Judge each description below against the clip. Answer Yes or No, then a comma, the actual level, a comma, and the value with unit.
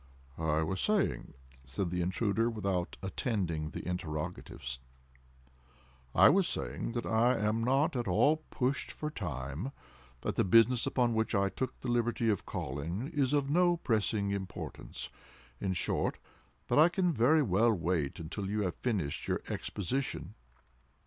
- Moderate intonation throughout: No, wide, 7.8 semitones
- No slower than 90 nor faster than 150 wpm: Yes, average, 140 wpm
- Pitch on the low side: Yes, low, 100 Hz